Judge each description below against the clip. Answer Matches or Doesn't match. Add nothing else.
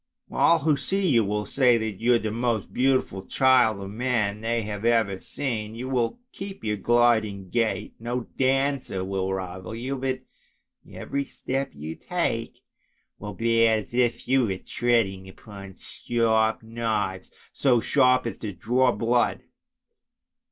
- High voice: Doesn't match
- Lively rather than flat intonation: Doesn't match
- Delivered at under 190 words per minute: Matches